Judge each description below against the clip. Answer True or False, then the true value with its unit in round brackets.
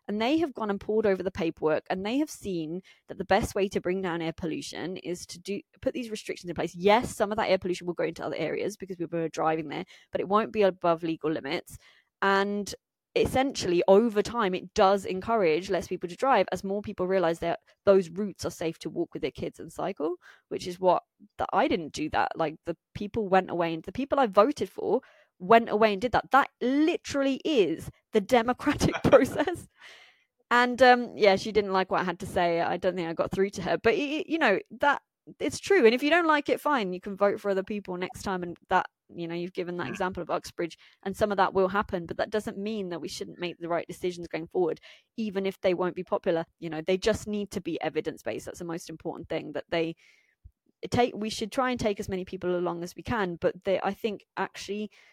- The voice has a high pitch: True (195 Hz)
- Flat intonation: False (3.9 semitones)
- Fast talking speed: True (240 wpm)